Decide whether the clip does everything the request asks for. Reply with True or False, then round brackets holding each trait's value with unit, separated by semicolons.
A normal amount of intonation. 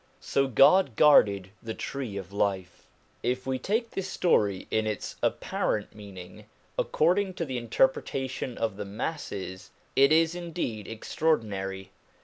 False (7.5 semitones)